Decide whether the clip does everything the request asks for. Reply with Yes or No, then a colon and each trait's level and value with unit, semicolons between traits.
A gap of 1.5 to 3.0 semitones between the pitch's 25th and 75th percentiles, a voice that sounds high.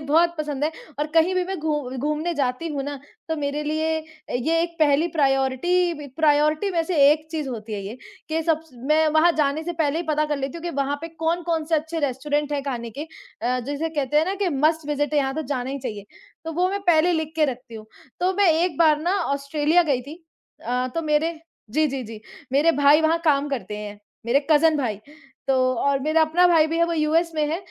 Yes: average, 2.7 semitones; very high, 305 Hz